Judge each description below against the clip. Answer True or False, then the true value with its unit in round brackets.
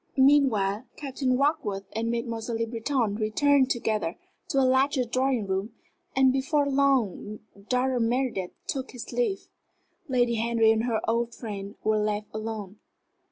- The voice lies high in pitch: True (235 Hz)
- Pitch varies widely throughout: False (3.6 semitones)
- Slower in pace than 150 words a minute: True (140 wpm)